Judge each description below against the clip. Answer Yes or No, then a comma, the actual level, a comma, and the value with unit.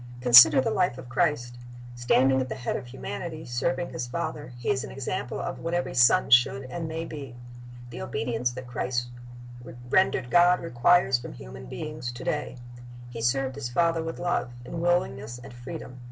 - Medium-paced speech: Yes, average, 180 wpm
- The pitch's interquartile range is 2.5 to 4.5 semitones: No, average, 5.0 semitones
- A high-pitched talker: No, low, 130 Hz